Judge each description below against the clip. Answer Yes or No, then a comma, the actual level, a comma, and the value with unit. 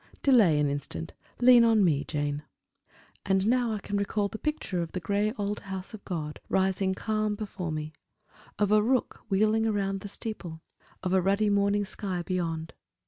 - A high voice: Yes, high, 200 Hz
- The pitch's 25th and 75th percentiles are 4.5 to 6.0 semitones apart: No, average, 3.5 semitones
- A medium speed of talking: Yes, average, 175 wpm